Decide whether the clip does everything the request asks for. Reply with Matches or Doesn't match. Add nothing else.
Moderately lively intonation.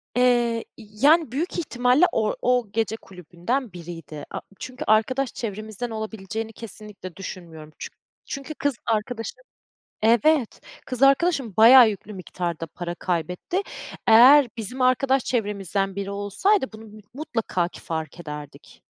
Matches